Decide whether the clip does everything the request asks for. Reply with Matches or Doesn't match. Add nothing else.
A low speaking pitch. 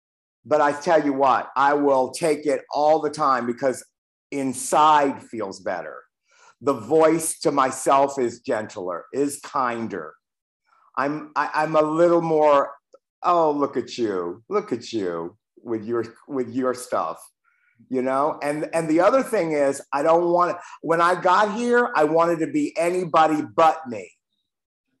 Doesn't match